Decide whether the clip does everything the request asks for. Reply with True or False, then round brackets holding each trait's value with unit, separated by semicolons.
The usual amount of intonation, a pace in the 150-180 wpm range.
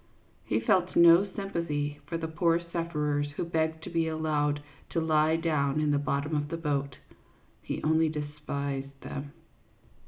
False (2.3 semitones; 155 wpm)